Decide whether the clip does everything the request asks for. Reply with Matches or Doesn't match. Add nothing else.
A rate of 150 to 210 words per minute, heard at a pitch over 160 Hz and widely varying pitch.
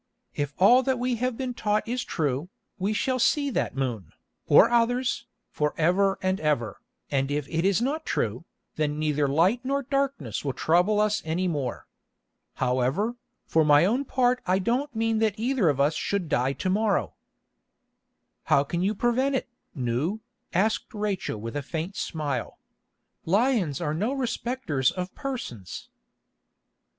Matches